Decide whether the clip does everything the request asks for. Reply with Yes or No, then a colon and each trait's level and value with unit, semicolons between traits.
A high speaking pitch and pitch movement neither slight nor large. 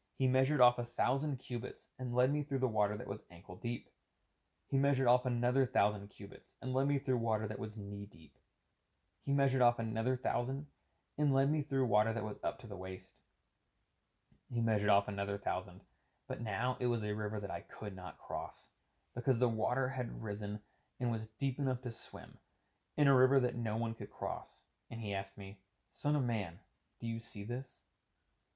No: low, 120 Hz; average, 3.9 semitones